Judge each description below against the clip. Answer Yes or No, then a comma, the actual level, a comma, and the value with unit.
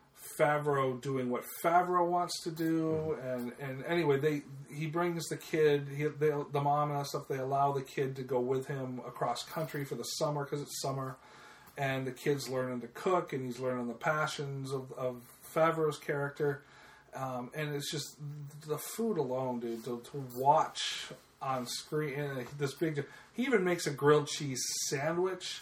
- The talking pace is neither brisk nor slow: Yes, average, 180 wpm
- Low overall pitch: No, medium, 145 Hz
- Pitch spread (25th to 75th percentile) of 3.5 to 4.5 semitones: No, average, 2.7 semitones